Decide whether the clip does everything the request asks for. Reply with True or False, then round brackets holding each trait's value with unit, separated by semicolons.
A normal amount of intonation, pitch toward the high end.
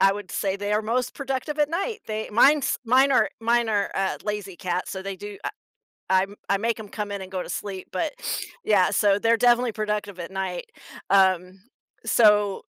True (3.3 semitones; 205 Hz)